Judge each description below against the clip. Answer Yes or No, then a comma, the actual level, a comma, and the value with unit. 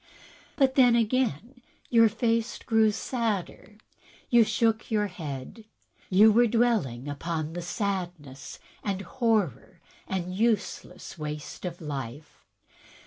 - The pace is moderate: No, slow, 110 wpm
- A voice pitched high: Yes, high, 205 Hz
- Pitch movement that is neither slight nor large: No, wide, 5.7 semitones